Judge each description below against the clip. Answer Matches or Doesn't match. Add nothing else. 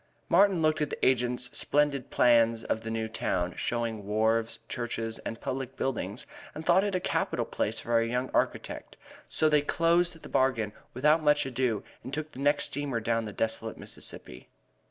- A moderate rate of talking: Matches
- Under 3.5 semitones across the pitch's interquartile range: Doesn't match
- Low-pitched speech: Matches